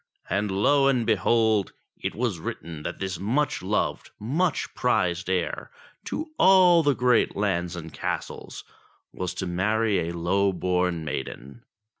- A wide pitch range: Yes, wide, 5.7 semitones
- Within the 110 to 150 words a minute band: Yes, average, 140 wpm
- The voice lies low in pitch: Yes, low, 100 Hz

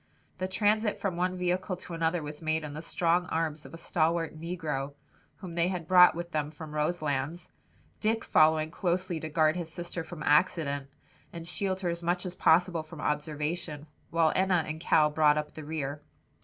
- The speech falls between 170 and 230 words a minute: Yes, average, 185 wpm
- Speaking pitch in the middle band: Yes, medium, 165 Hz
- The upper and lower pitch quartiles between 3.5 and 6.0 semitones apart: No, narrow, 2.5 semitones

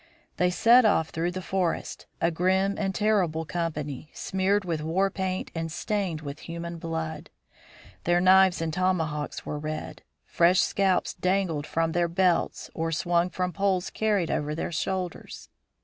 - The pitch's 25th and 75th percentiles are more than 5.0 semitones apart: No, average, 2.7 semitones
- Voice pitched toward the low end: No, medium, 175 Hz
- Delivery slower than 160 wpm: Yes, average, 150 wpm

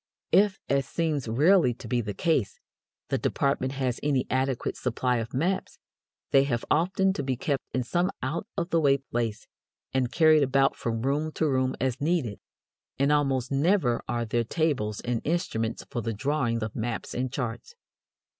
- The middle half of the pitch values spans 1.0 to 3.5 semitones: No, average, 4.4 semitones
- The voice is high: No, low, 135 Hz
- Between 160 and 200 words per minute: Yes, average, 175 wpm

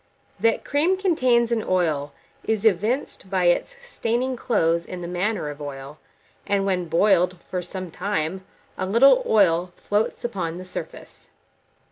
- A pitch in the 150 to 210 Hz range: Yes, high, 190 Hz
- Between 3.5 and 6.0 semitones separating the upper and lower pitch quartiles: Yes, average, 4.9 semitones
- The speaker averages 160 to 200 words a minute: No, average, 145 wpm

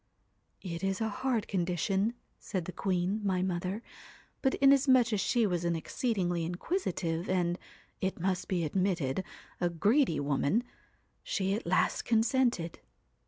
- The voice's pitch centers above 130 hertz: Yes, high, 190 Hz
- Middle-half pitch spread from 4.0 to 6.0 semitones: Yes, average, 4.3 semitones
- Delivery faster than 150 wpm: No, slow, 135 wpm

